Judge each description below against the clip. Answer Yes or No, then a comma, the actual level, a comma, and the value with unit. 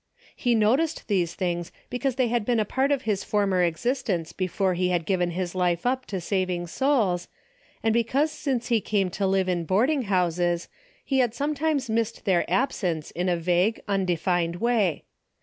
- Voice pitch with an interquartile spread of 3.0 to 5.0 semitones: No, wide, 5.4 semitones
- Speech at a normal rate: Yes, average, 175 wpm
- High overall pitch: Yes, high, 195 Hz